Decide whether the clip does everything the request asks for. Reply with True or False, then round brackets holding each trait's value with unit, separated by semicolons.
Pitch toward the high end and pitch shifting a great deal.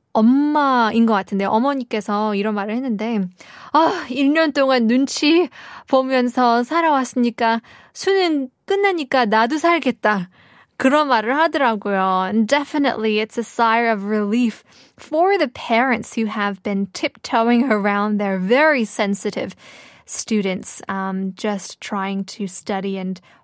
False (230 Hz; 4.8 semitones)